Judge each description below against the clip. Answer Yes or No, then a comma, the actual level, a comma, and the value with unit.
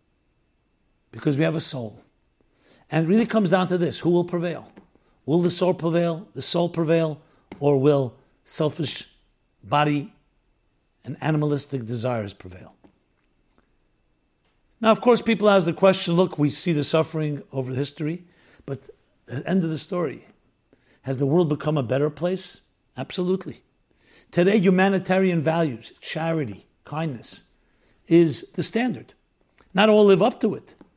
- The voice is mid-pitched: Yes, medium, 160 Hz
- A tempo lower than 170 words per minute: Yes, average, 140 wpm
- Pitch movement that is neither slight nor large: Yes, average, 4.5 semitones